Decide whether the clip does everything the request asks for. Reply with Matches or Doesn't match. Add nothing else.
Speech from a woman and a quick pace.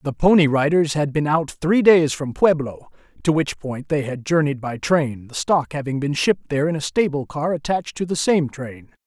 Doesn't match